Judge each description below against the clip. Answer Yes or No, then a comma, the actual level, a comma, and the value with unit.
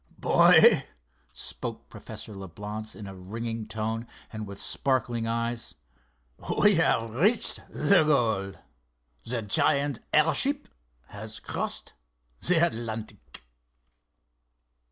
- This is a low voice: Yes, low, 115 Hz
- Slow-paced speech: Yes, slow, 95 wpm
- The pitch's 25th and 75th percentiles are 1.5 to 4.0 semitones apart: No, average, 4.5 semitones